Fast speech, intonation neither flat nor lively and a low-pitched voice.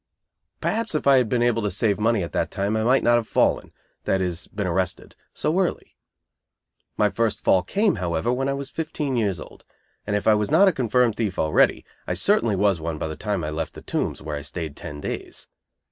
No: fast, 220 wpm; wide, 5.7 semitones; low, 105 Hz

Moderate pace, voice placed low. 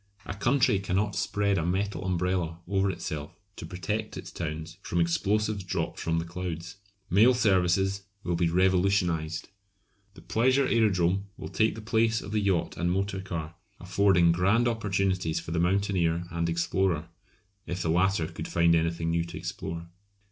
Yes: average, 160 wpm; very low, 90 Hz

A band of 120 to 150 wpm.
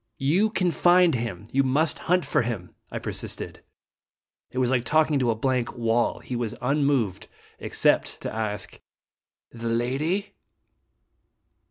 Yes: average, 145 wpm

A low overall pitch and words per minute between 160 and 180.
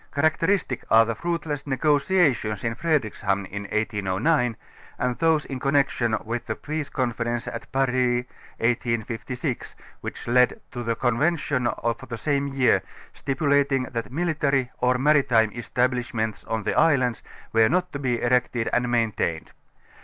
No: low, 125 Hz; average, 140 wpm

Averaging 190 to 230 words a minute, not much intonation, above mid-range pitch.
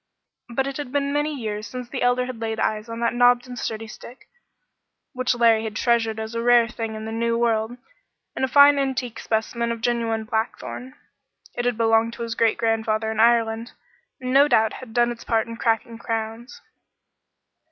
Yes: average, 195 wpm; narrow, 1.8 semitones; high, 235 Hz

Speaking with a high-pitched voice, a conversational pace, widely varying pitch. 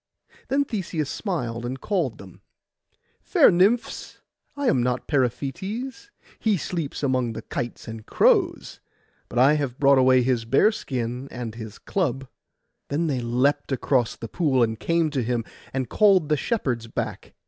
No: low, 135 Hz; average, 150 wpm; wide, 5.8 semitones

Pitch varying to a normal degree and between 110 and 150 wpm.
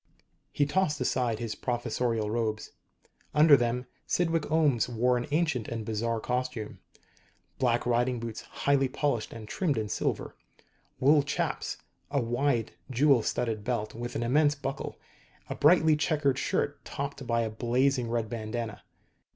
Yes: average, 3.6 semitones; average, 145 wpm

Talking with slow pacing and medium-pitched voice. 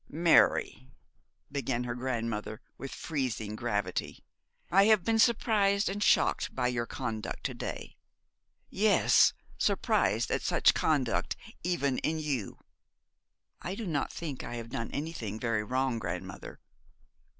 No: slow, 130 wpm; low, 130 Hz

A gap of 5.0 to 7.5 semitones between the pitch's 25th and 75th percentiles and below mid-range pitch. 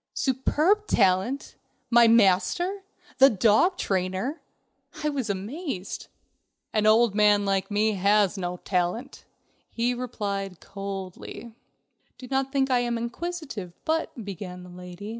No: wide, 5.4 semitones; high, 215 Hz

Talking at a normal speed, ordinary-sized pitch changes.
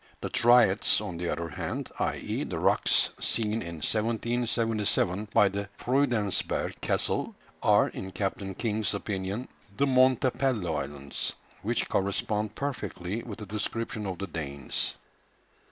No: slow, 125 wpm; average, 3.7 semitones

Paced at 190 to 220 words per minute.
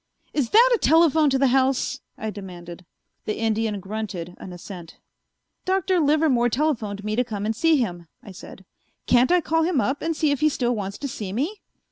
Yes: average, 195 wpm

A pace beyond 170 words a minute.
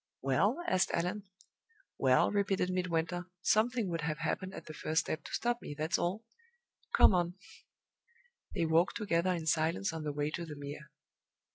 No: average, 165 wpm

